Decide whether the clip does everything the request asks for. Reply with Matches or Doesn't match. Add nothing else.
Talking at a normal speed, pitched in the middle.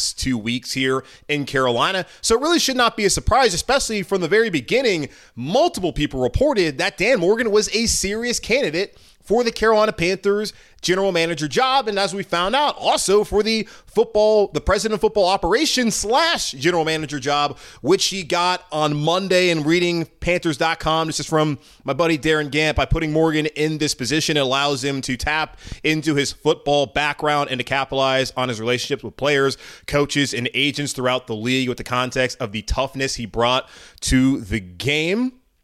Matches